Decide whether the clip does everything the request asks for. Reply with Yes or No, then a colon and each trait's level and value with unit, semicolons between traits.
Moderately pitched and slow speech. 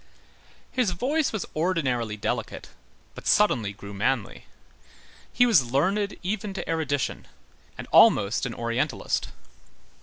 Yes: medium, 155 Hz; slow, 115 wpm